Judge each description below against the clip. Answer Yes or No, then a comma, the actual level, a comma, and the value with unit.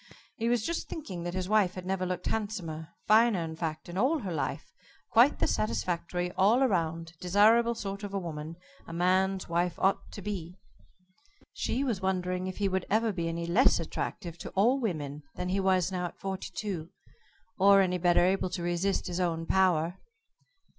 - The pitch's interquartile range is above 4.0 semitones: No, average, 2.7 semitones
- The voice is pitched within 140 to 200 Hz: Yes, medium, 185 Hz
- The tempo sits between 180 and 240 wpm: Yes, average, 185 wpm